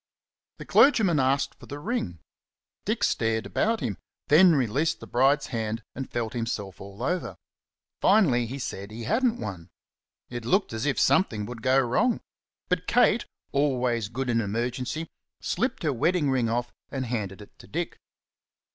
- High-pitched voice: No, low, 125 Hz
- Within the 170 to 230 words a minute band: No, average, 160 wpm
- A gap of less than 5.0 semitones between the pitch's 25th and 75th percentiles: No, wide, 5.5 semitones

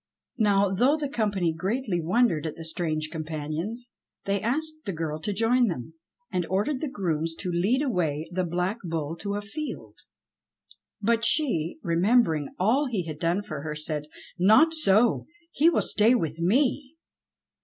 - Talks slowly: No, average, 160 wpm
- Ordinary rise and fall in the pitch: No, wide, 6.6 semitones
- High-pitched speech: Yes, high, 195 Hz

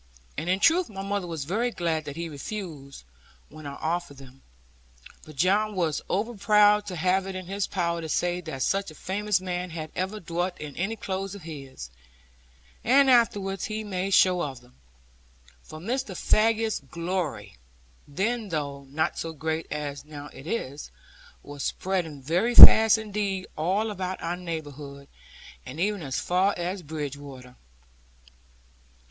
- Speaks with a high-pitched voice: No, medium, 175 Hz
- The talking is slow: No, average, 155 wpm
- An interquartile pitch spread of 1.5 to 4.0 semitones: No, average, 4.9 semitones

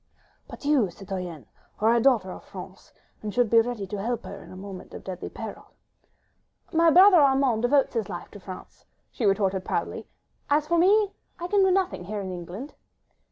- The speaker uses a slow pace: No, average, 190 wpm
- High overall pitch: Yes, high, 225 Hz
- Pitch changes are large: Yes, wide, 7.2 semitones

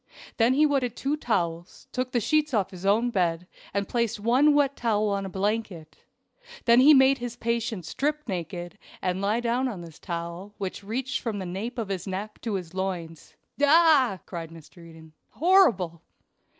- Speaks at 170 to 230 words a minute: Yes, average, 175 wpm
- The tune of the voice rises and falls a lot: Yes, wide, 5.7 semitones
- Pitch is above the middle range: Yes, high, 210 Hz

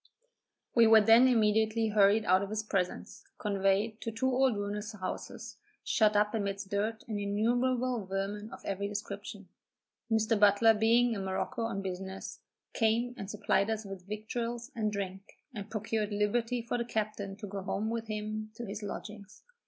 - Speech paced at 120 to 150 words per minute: No, average, 165 wpm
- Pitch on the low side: No, high, 215 Hz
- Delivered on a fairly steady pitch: Yes, narrow, 2.0 semitones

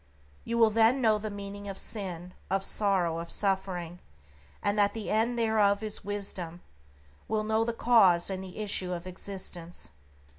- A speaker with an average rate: Yes, average, 160 wpm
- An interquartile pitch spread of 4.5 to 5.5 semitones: No, average, 3.0 semitones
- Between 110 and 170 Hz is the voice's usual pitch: No, high, 200 Hz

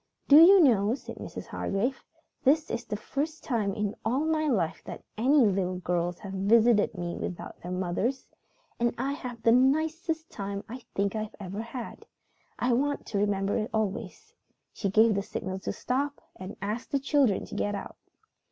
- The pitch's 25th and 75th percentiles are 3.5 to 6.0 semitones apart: Yes, wide, 5.5 semitones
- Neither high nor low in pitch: No, high, 225 Hz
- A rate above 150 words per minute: Yes, average, 180 wpm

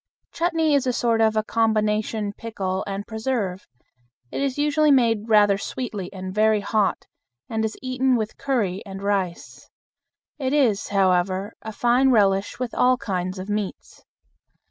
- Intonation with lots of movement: No, average, 4.2 semitones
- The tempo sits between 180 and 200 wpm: No, average, 150 wpm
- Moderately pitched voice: No, high, 215 Hz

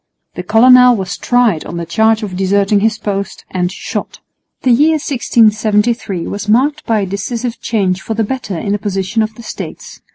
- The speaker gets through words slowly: No, average, 185 wpm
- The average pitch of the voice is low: No, high, 215 Hz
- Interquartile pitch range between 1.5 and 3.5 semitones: Yes, average, 3.1 semitones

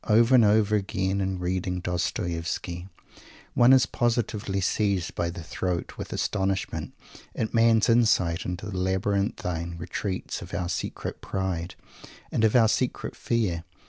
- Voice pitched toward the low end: Yes, very low, 95 Hz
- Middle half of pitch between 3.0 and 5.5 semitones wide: Yes, average, 3.7 semitones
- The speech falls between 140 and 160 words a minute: Yes, average, 145 wpm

